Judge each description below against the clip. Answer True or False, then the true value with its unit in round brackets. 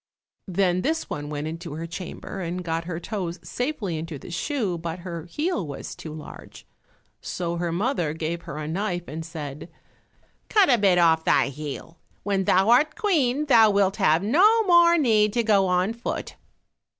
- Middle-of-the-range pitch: True (180 Hz)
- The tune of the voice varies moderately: False (5.8 semitones)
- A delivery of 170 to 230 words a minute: True (175 wpm)